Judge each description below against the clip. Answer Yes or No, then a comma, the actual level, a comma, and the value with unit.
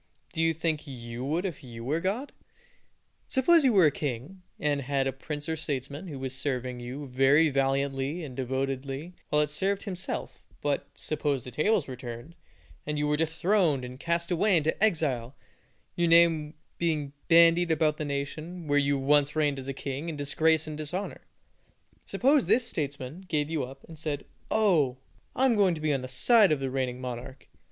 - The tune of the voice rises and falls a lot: No, average, 3.7 semitones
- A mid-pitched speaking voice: Yes, medium, 150 Hz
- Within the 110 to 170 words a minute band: No, average, 185 wpm